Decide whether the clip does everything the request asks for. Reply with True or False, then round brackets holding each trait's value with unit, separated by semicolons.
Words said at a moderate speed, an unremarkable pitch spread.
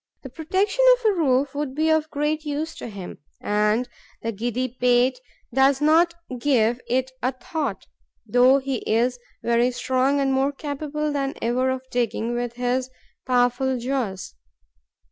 True (150 wpm; 3.0 semitones)